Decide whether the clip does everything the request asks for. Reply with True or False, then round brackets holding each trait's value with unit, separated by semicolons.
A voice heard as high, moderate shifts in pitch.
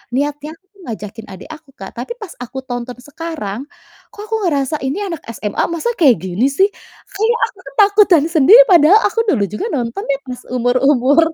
False (285 Hz; 6.0 semitones)